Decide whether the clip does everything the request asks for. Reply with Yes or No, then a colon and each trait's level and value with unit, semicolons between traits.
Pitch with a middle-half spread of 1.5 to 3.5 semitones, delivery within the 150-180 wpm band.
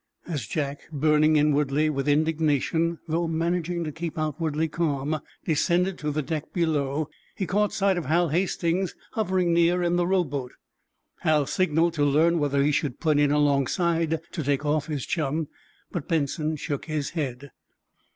Yes: narrow, 2.6 semitones; average, 160 wpm